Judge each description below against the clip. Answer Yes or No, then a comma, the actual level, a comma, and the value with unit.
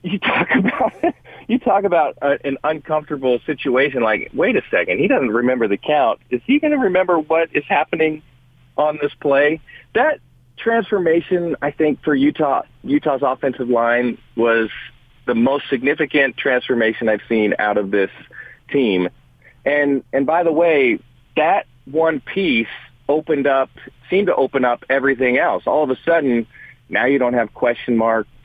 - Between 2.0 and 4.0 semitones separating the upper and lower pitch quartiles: No, average, 4.7 semitones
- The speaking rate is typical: Yes, average, 160 wpm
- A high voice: No, medium, 140 Hz